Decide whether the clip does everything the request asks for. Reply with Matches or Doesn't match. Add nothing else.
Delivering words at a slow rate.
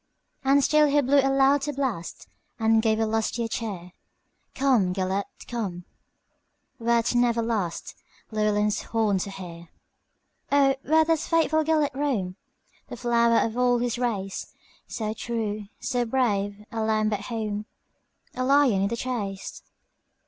Matches